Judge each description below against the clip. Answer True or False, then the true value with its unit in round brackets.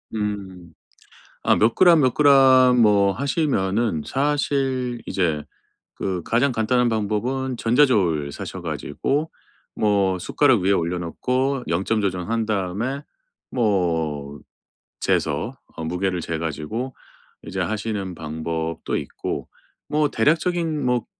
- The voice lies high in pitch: False (110 Hz)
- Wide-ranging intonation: True (6.4 semitones)